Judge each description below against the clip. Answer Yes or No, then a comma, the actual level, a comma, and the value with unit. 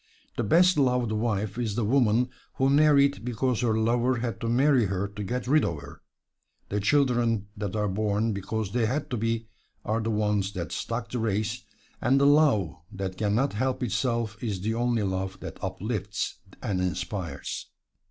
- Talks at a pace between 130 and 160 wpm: No, average, 180 wpm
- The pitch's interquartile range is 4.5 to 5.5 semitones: No, average, 3.4 semitones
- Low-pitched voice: Yes, low, 110 Hz